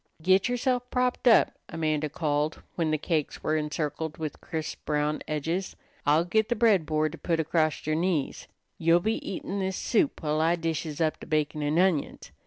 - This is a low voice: No, medium, 160 Hz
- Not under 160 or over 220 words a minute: Yes, average, 185 wpm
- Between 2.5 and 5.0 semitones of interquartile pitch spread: Yes, average, 3.5 semitones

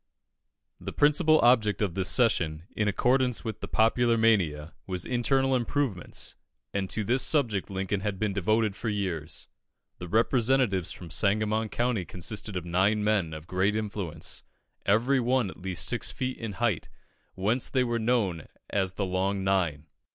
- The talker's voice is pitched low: Yes, low, 105 Hz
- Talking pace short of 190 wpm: Yes, average, 160 wpm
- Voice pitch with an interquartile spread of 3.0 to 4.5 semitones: Yes, average, 4.1 semitones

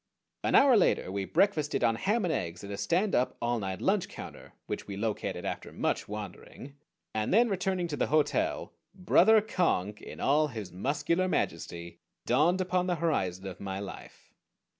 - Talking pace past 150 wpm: Yes, average, 175 wpm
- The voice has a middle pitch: Yes, medium, 145 Hz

